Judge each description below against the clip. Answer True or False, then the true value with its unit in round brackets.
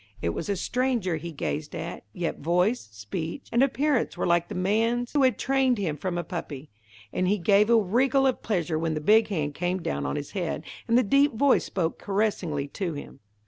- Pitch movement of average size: False (6.3 semitones)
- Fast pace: True (210 wpm)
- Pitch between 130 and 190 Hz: True (185 Hz)